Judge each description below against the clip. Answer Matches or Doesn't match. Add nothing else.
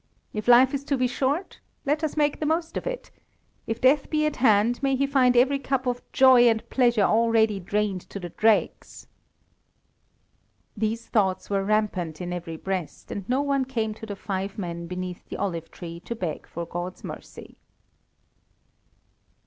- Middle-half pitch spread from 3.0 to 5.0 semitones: Doesn't match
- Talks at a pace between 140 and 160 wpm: Doesn't match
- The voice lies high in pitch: Matches